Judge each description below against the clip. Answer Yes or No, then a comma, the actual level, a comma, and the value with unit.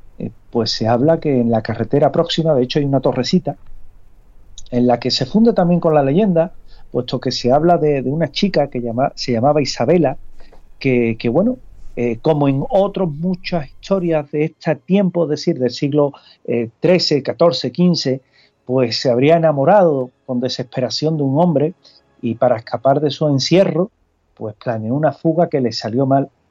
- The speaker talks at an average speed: Yes, average, 175 wpm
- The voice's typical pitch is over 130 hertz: Yes, medium, 140 Hz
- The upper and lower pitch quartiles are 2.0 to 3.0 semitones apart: No, average, 5.1 semitones